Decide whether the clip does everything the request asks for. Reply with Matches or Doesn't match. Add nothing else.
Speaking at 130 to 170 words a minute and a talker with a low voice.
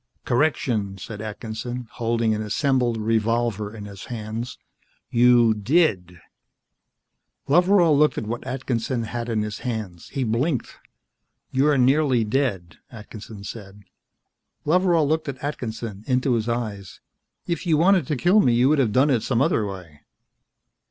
Matches